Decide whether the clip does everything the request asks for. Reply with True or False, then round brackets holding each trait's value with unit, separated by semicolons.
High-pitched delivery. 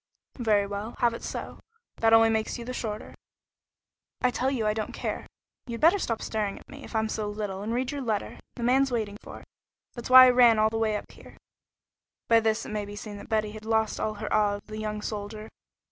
True (220 Hz)